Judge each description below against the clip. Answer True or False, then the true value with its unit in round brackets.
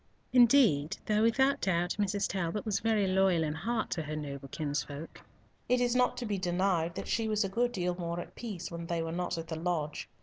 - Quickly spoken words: True (215 wpm)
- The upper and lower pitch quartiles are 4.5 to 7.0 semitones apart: True (4.9 semitones)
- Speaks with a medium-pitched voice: True (180 Hz)